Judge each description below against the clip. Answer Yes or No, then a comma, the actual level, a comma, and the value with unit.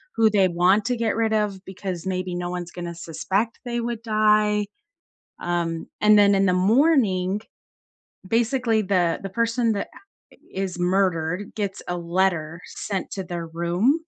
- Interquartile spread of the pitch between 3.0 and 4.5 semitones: Yes, average, 3.6 semitones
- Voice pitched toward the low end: No, high, 195 Hz